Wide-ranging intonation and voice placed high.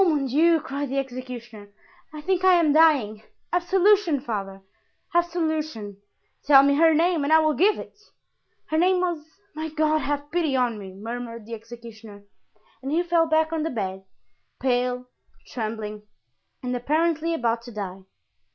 Yes: wide, 5.9 semitones; very high, 285 Hz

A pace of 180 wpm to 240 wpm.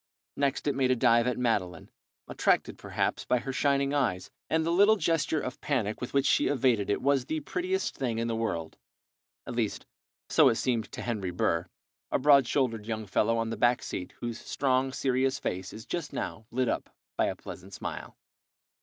Yes: average, 195 wpm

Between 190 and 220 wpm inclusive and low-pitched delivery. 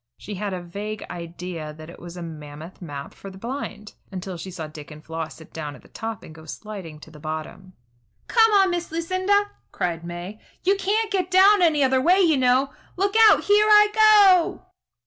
No: fast, 205 wpm; high, 205 Hz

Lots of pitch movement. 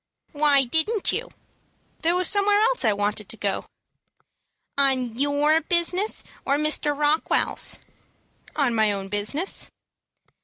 Yes: wide, 6.8 semitones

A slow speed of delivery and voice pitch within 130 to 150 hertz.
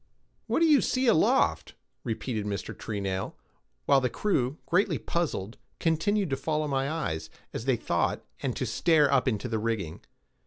No: average, 160 wpm; low, 135 Hz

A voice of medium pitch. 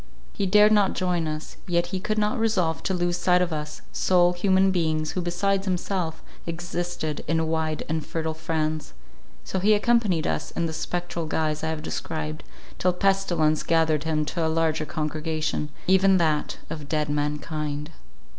Yes: medium, 165 Hz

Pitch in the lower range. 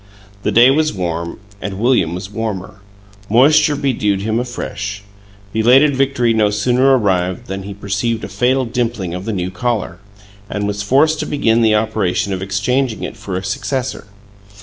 Yes: low, 110 Hz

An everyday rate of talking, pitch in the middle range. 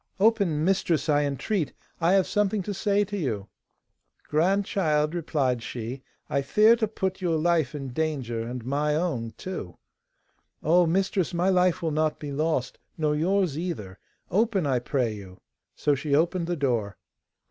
Yes: average, 160 wpm; medium, 155 Hz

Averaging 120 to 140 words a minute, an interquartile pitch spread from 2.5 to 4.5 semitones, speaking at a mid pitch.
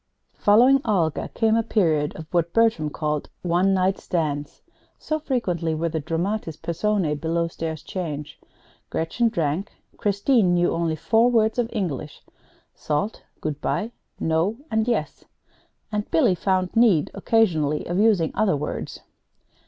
No: slow, 135 wpm; wide, 5.4 semitones; medium, 175 Hz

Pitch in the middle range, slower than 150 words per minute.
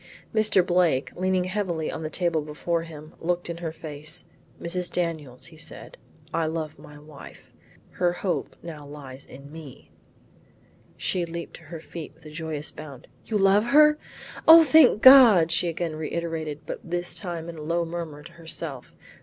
No: medium, 165 Hz; average, 170 wpm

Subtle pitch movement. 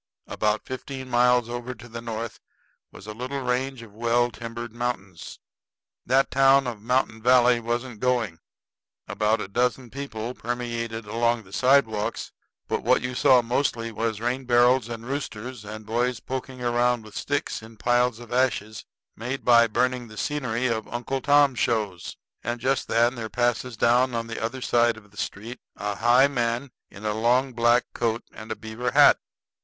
Yes: narrow, 2.0 semitones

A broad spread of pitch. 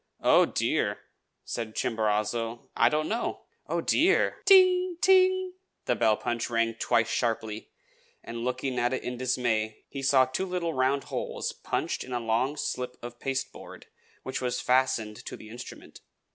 No: average, 3.2 semitones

